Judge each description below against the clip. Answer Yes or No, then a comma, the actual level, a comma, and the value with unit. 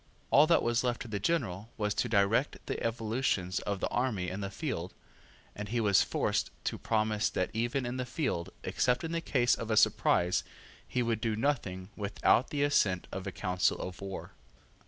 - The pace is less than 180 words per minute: No, average, 195 wpm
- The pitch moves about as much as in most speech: Yes, average, 4.1 semitones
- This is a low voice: Yes, low, 110 Hz